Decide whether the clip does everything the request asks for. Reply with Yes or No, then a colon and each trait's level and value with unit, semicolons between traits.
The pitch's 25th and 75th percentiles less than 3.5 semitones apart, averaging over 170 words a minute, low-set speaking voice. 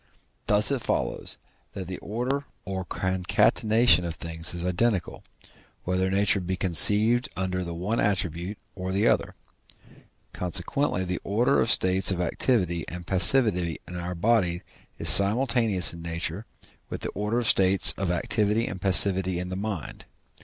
No: average, 3.1 semitones; average, 150 wpm; very low, 95 Hz